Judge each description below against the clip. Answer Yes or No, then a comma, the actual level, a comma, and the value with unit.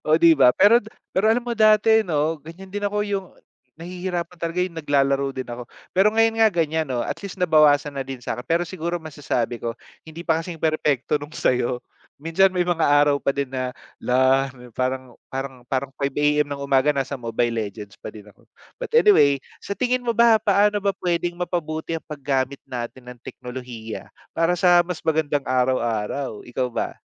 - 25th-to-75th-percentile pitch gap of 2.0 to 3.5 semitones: No, wide, 5.5 semitones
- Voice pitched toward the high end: No, medium, 150 Hz